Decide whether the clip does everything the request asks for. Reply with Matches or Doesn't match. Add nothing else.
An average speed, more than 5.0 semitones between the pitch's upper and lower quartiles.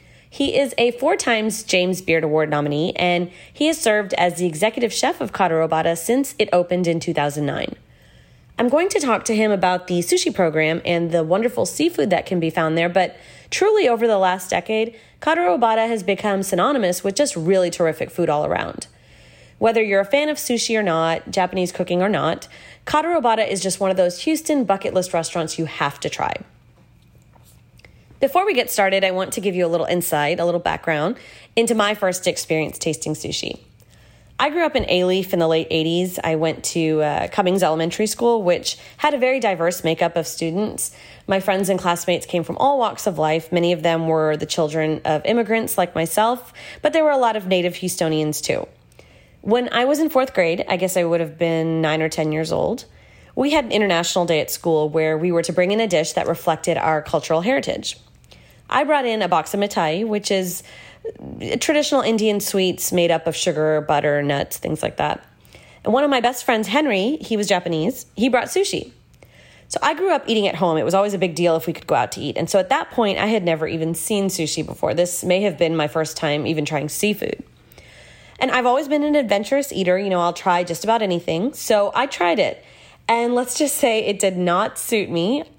Doesn't match